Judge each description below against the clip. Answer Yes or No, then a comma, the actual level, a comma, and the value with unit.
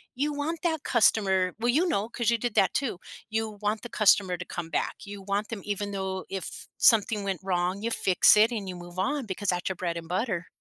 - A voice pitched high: Yes, high, 205 Hz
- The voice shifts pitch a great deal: No, average, 3.7 semitones